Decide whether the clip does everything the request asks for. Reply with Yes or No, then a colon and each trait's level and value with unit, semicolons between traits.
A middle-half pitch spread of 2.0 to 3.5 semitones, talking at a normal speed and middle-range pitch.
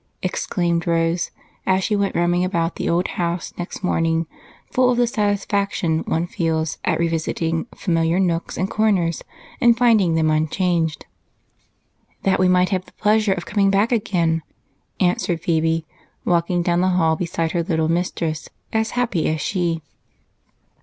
Yes: average, 2.9 semitones; average, 150 wpm; medium, 175 Hz